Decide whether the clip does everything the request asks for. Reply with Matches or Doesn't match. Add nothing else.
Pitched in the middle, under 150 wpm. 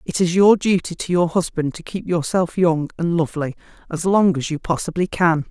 Doesn't match